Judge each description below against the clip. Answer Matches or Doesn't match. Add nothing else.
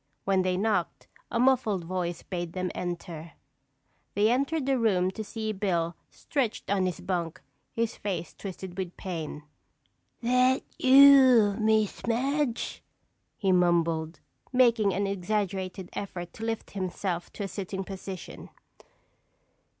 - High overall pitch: Matches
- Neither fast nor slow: Doesn't match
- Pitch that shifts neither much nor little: Matches